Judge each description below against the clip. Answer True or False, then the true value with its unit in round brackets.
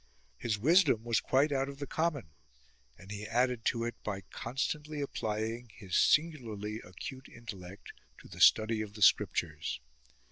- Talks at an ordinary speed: True (150 wpm)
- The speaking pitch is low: True (115 Hz)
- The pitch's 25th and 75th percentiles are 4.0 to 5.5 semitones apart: True (4.5 semitones)